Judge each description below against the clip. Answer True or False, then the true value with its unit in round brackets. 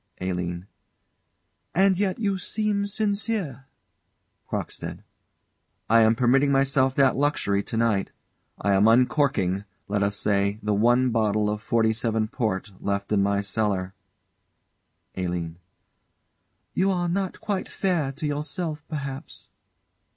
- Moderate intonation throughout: False (7.1 semitones)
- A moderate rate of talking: False (120 wpm)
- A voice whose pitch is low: True (115 Hz)